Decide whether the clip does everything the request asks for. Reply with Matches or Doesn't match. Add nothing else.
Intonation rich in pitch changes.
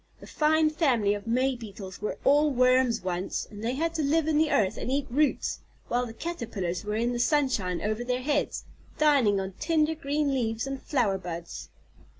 Matches